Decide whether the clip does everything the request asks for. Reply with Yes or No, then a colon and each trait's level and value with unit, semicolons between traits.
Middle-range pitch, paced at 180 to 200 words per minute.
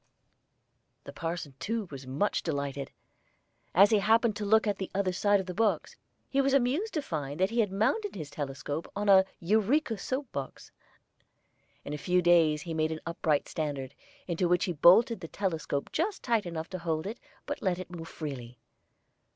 Yes: medium, 180 Hz; average, 185 wpm